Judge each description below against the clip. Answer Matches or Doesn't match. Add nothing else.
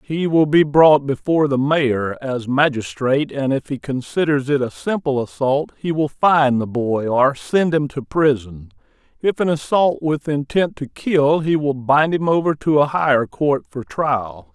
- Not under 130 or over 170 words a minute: Doesn't match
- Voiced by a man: Matches